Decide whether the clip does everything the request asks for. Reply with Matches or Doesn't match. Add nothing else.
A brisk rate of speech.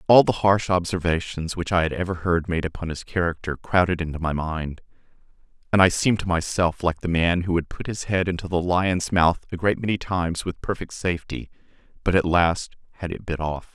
Matches